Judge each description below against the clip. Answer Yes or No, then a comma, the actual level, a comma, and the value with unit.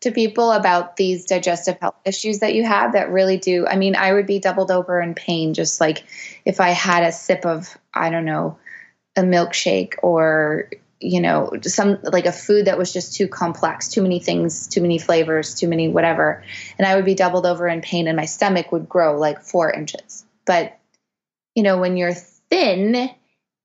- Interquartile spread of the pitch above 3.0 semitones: No, average, 2.7 semitones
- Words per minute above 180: Yes, average, 200 wpm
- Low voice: No, medium, 180 Hz